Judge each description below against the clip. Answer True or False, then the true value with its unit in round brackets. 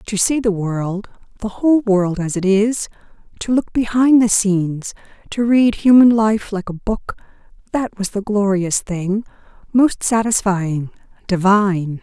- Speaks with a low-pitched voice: False (205 Hz)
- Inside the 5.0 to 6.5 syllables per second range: False (4.2 syllables/s)